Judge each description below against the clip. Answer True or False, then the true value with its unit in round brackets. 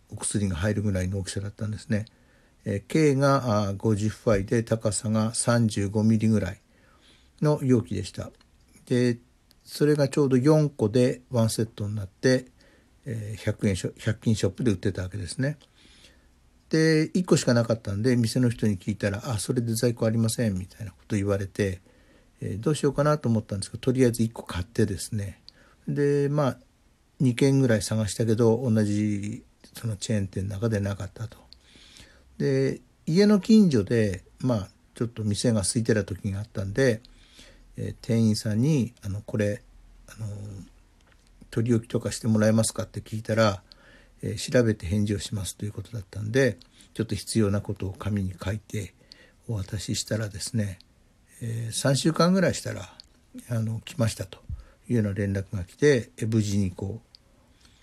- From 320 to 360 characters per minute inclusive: True (330 characters per minute)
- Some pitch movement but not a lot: True (3.2 semitones)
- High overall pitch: False (110 Hz)